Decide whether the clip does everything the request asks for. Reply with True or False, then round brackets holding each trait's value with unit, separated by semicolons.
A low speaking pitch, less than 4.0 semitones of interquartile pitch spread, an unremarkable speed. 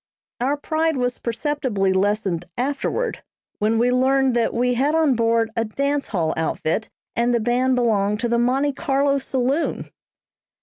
False (245 Hz; 3.6 semitones; 150 wpm)